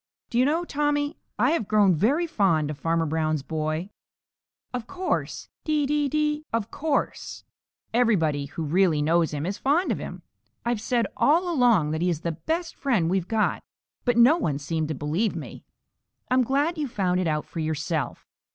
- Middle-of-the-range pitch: No, high, 210 Hz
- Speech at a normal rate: Yes, average, 180 wpm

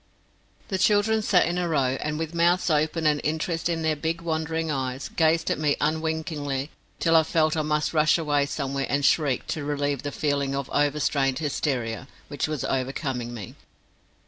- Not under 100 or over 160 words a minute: No, average, 175 wpm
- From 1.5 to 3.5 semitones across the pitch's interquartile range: Yes, narrow, 2.5 semitones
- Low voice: No, medium, 150 Hz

